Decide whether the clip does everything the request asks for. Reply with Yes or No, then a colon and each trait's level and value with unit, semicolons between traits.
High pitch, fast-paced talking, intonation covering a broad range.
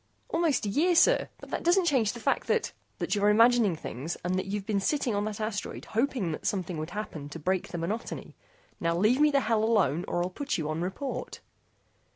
Yes: high, 210 Hz; fast, 220 wpm; wide, 5.7 semitones